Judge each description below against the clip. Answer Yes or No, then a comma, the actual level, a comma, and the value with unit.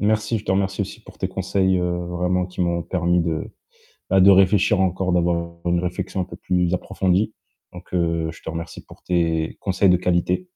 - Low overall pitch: Yes, very low, 90 Hz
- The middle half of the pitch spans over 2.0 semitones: No, narrow, 1.7 semitones